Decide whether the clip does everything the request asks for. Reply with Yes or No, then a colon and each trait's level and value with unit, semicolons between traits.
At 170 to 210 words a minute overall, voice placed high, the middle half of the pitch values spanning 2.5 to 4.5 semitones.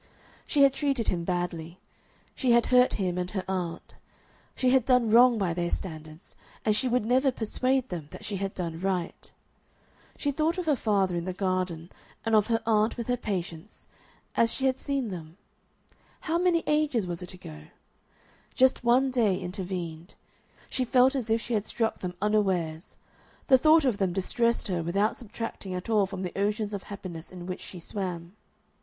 No: average, 185 wpm; high, 205 Hz; wide, 5.6 semitones